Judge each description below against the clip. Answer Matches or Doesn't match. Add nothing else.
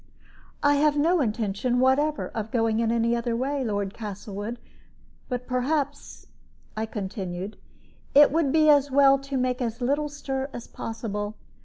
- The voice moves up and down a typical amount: Matches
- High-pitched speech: Matches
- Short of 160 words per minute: Matches